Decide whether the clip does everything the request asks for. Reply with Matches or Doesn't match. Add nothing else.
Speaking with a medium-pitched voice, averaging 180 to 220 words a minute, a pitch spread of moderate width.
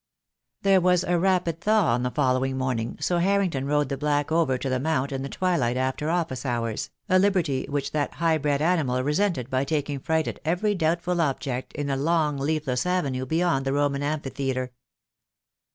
Matches